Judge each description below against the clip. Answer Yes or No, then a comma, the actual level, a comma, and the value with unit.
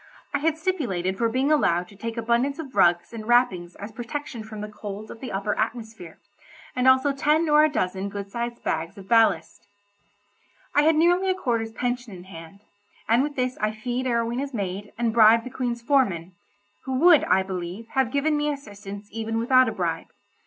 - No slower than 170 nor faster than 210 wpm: Yes, average, 190 wpm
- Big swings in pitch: No, average, 4.6 semitones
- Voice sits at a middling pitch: No, high, 230 Hz